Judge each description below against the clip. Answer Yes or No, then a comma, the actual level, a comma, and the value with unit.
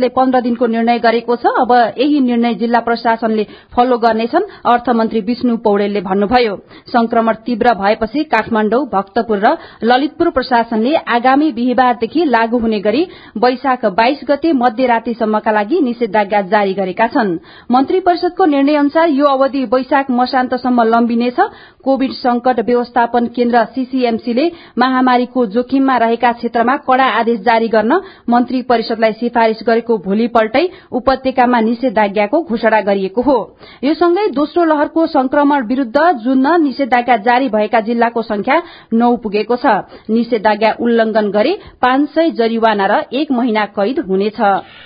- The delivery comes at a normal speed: No, slow, 130 wpm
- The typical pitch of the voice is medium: No, high, 245 Hz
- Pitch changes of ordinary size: Yes, average, 3.0 semitones